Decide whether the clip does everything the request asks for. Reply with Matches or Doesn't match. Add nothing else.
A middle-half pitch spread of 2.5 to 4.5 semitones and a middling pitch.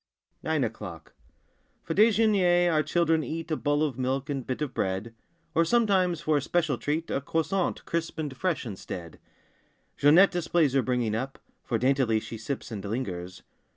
Doesn't match